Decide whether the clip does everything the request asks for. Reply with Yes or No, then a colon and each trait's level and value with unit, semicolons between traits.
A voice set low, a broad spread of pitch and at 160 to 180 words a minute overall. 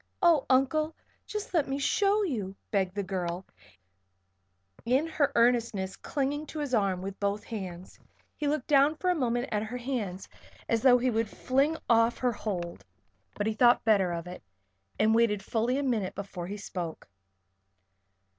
No: high, 230 Hz; wide, 5.9 semitones; average, 165 wpm